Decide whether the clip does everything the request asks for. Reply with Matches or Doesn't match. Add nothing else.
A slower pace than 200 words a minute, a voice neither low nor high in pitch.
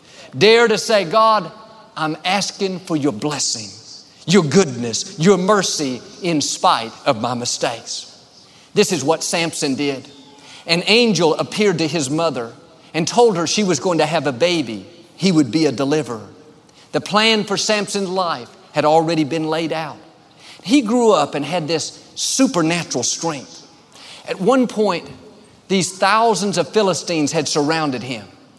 Matches